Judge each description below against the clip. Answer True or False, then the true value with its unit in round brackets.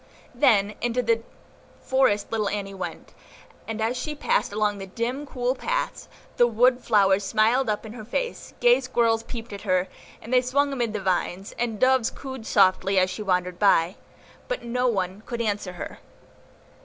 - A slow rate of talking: False (170 wpm)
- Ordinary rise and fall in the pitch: True (4.0 semitones)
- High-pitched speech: True (225 Hz)